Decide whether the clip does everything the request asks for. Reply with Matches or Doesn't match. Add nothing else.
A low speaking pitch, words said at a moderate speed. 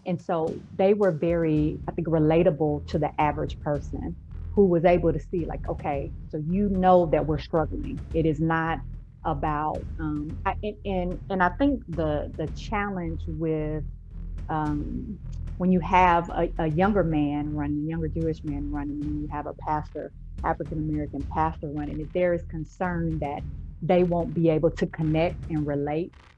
Doesn't match